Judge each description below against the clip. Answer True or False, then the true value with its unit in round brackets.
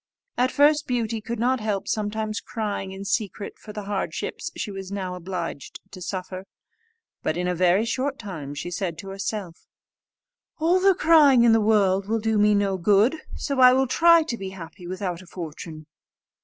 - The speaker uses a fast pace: False (185 wpm)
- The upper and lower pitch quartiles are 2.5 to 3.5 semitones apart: False (4.2 semitones)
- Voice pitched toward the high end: True (205 Hz)